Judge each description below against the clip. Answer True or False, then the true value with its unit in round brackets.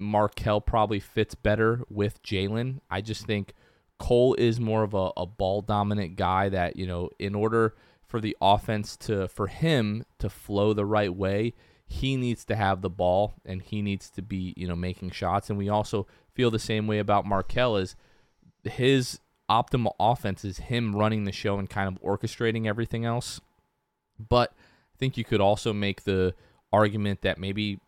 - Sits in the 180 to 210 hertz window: False (105 Hz)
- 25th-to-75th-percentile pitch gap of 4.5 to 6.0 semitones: False (2.6 semitones)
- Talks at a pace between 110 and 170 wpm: False (180 wpm)